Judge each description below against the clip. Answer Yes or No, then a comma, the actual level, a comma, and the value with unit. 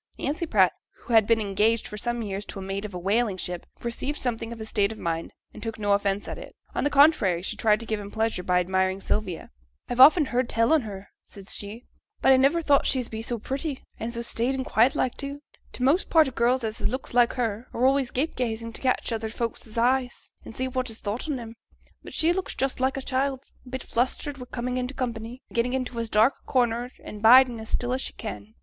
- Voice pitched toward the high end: Yes, high, 235 Hz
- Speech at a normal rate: No, fast, 245 wpm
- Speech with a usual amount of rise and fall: Yes, average, 3.4 semitones